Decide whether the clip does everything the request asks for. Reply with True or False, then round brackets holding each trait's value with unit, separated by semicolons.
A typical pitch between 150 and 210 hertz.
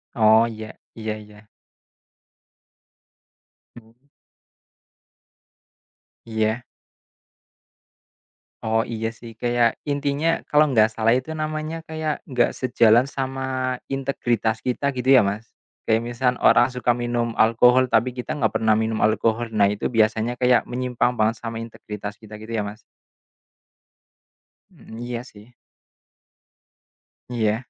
False (115 Hz)